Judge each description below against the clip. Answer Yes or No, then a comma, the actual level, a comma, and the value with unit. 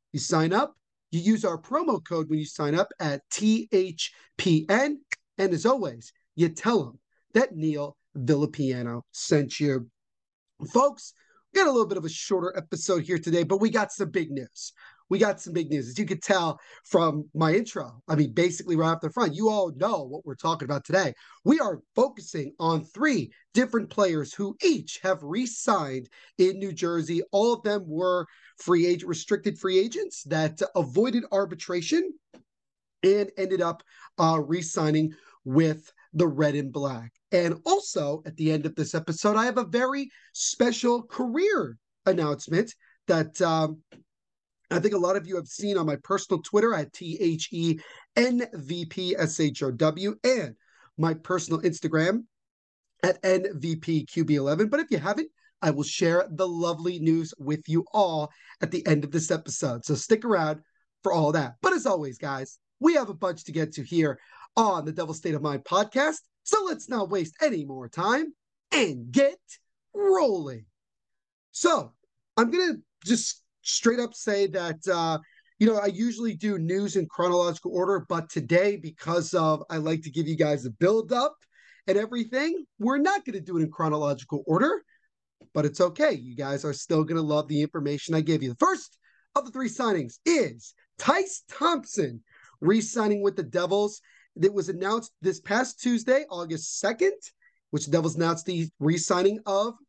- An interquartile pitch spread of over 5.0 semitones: Yes, wide, 5.6 semitones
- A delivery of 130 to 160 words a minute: No, average, 170 wpm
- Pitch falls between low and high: Yes, medium, 180 Hz